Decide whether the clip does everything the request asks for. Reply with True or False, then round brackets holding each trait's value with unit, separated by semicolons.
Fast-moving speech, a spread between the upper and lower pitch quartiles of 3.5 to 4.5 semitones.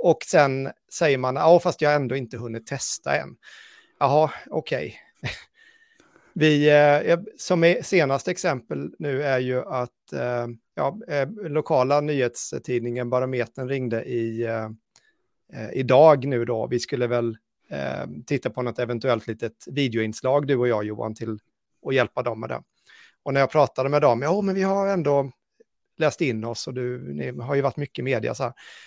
False (160 wpm; 3.8 semitones)